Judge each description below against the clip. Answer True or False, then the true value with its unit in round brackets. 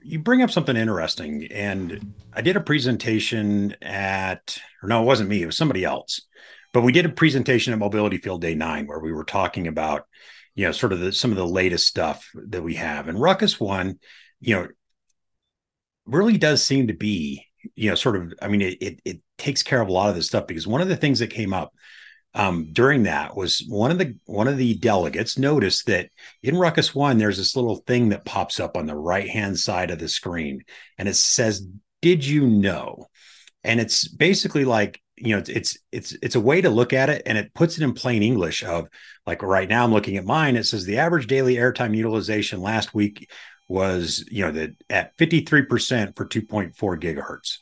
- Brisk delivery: True (215 wpm)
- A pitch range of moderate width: False (5.7 semitones)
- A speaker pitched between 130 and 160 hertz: False (110 Hz)